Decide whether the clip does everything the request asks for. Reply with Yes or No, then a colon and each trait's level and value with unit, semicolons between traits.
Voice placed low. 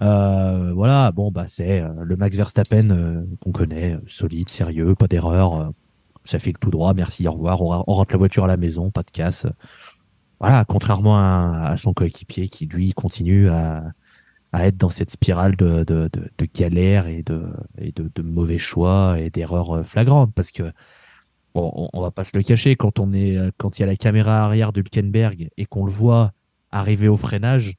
Yes: very low, 95 Hz